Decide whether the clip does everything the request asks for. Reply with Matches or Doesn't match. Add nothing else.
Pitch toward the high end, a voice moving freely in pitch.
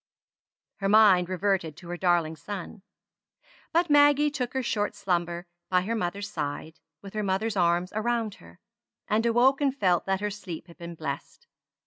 Doesn't match